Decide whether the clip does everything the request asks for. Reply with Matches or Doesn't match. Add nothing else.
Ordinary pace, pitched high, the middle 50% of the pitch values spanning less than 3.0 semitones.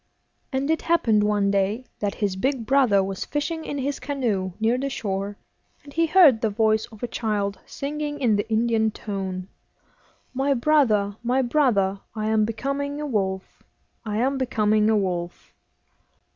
Doesn't match